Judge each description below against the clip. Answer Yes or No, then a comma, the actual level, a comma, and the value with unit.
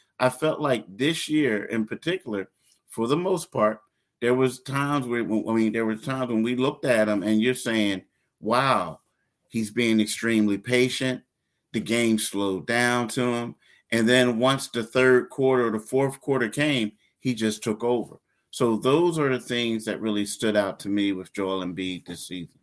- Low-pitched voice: Yes, low, 115 Hz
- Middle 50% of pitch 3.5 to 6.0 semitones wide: No, average, 3.1 semitones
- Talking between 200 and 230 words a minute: No, average, 185 wpm